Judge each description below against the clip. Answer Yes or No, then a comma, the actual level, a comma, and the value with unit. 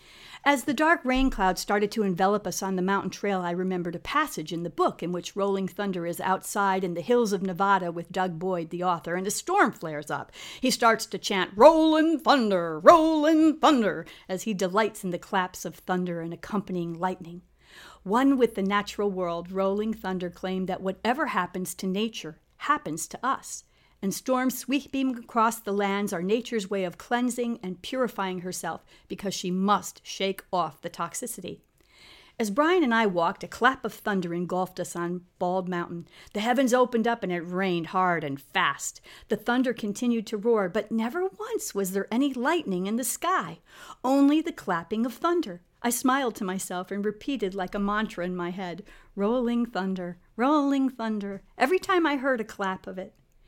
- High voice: Yes, high, 200 Hz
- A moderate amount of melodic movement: Yes, average, 5.0 semitones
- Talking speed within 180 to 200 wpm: Yes, average, 185 wpm